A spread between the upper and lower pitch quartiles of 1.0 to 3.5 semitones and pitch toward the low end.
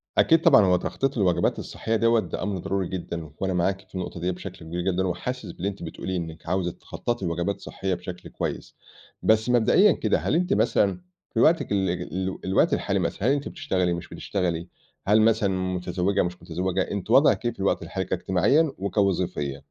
Yes: average, 3.1 semitones; very low, 95 Hz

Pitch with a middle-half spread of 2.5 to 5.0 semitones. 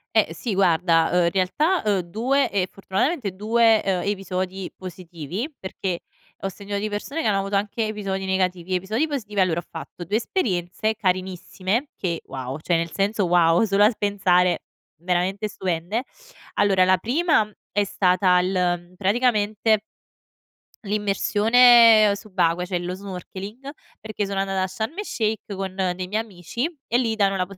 Yes: average, 2.9 semitones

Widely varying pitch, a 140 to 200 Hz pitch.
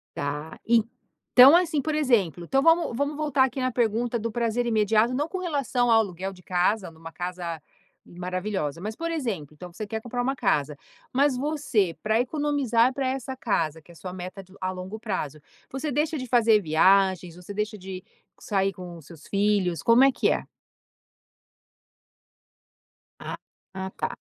No: wide, 6.2 semitones; high, 215 Hz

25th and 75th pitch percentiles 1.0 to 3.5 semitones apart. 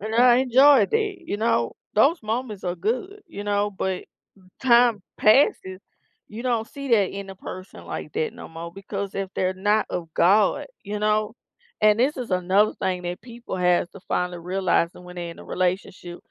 No: average, 4.4 semitones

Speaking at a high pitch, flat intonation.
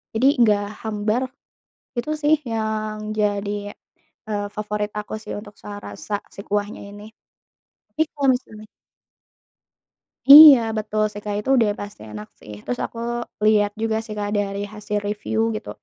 Yes: high, 210 Hz; narrow, 1.1 semitones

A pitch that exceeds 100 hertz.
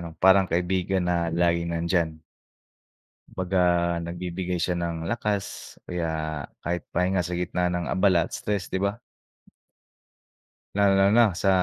No: very low, 90 Hz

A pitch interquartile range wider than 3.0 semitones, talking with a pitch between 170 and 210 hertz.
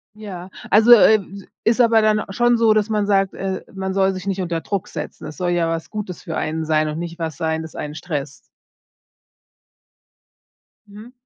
Yes: average, 4.5 semitones; high, 190 Hz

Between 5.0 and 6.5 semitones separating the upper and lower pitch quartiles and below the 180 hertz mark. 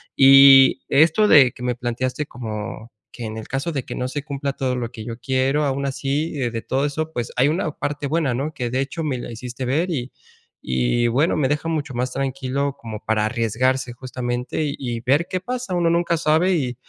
No: average, 3.4 semitones; low, 135 Hz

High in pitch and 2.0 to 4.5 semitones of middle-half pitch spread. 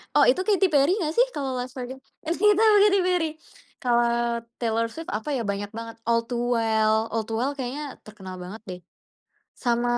No: high, 240 Hz; average, 5.0 semitones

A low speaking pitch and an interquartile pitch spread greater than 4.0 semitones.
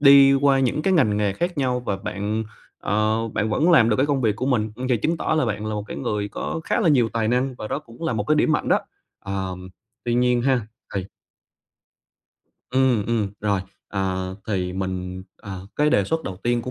Yes: low, 115 Hz; average, 4.8 semitones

